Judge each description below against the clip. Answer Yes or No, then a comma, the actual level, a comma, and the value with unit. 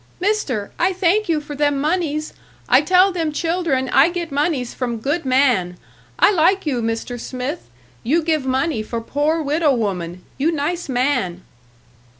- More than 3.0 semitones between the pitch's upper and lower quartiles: Yes, average, 5.1 semitones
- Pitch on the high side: Yes, very high, 290 Hz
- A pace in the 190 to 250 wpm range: No, average, 155 wpm